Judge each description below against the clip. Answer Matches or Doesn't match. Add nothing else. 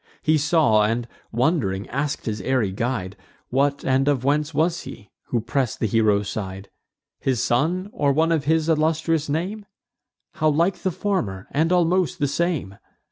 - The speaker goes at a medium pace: Matches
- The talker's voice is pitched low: Doesn't match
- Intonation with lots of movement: Matches